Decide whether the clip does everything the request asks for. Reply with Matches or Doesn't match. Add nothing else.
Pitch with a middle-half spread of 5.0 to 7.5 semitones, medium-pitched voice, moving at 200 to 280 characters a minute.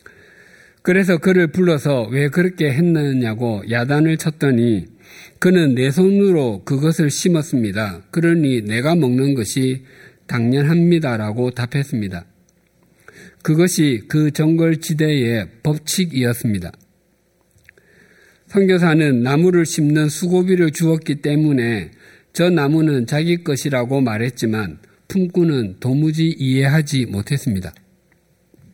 Matches